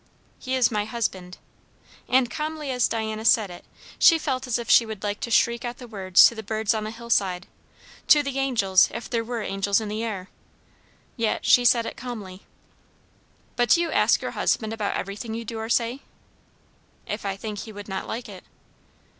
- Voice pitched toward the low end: No, high, 225 Hz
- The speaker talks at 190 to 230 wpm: Yes, average, 195 wpm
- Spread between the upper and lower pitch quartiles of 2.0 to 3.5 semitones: Yes, average, 2.9 semitones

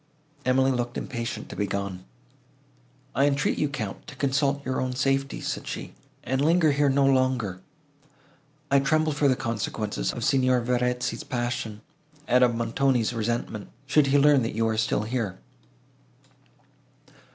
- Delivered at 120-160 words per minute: Yes, average, 150 wpm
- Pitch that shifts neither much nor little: Yes, average, 3.1 semitones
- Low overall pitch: Yes, low, 130 Hz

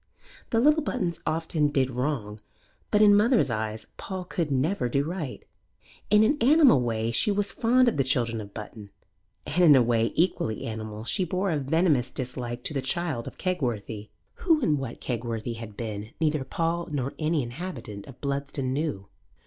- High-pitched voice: No, medium, 140 Hz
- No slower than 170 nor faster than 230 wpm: Yes, average, 180 wpm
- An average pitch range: No, wide, 7.2 semitones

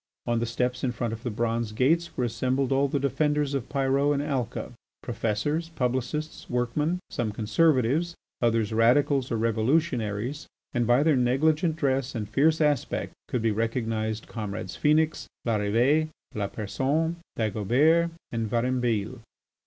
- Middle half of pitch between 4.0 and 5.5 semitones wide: Yes, average, 4.4 semitones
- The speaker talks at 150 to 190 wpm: No, slow, 135 wpm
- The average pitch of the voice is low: Yes, low, 125 Hz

